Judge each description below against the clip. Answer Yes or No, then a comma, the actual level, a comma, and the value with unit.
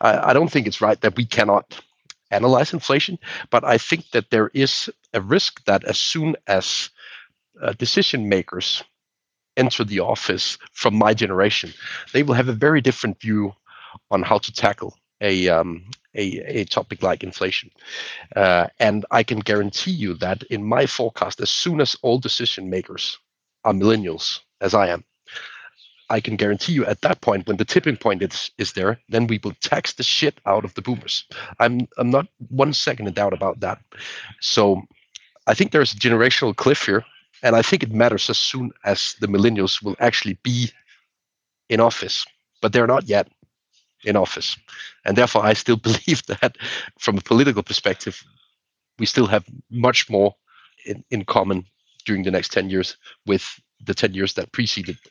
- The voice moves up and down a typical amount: Yes, average, 4.0 semitones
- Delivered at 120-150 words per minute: No, average, 175 wpm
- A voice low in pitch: Yes, low, 115 Hz